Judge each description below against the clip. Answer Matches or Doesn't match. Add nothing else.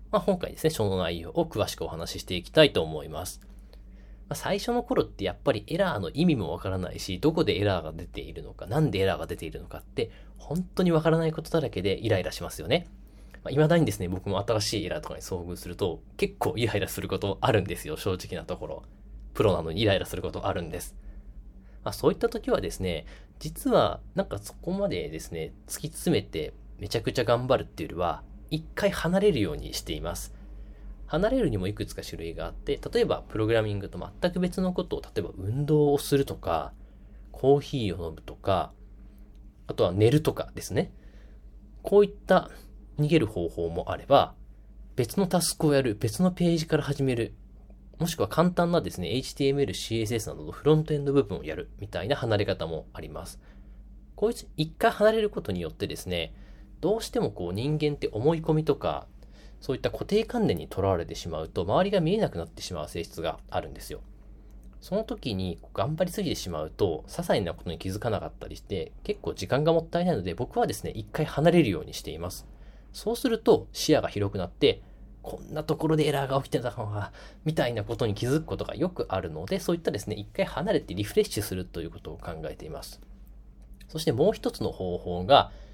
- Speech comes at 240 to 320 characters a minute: Doesn't match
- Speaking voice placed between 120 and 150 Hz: Doesn't match